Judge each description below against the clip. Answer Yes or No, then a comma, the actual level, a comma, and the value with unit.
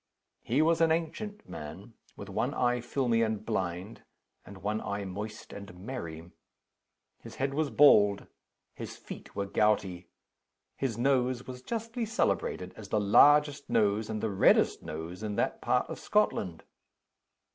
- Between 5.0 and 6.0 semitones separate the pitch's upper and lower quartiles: Yes, wide, 5.4 semitones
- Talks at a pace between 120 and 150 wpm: Yes, average, 145 wpm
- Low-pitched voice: Yes, low, 110 Hz